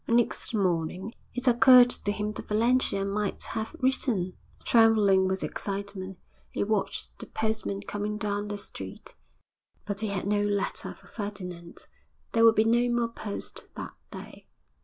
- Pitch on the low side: No, high, 210 Hz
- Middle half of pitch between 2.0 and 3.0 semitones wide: Yes, narrow, 2.4 semitones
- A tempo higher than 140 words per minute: Yes, average, 150 wpm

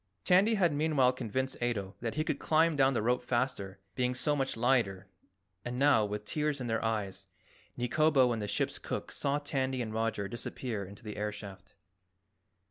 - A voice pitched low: Yes, low, 125 Hz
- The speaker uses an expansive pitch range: No, average, 4.6 semitones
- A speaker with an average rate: Yes, average, 180 wpm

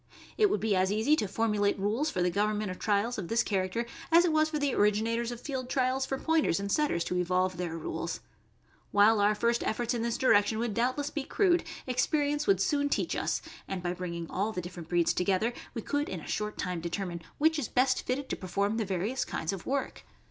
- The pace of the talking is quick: Yes, fast, 220 wpm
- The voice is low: No, high, 215 Hz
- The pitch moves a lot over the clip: Yes, wide, 5.8 semitones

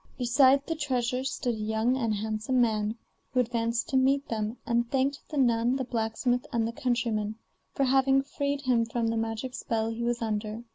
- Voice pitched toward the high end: Yes, high, 240 Hz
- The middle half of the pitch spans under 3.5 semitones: Yes, average, 2.8 semitones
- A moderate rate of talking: Yes, average, 190 wpm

